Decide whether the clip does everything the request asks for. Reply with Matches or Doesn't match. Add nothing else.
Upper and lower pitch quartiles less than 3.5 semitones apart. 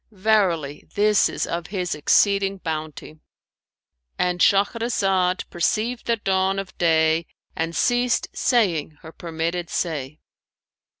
Doesn't match